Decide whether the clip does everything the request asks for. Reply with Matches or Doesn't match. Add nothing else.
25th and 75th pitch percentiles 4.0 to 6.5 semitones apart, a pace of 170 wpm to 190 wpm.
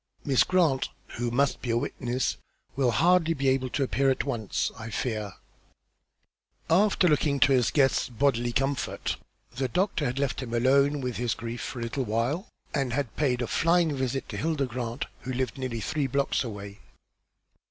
Doesn't match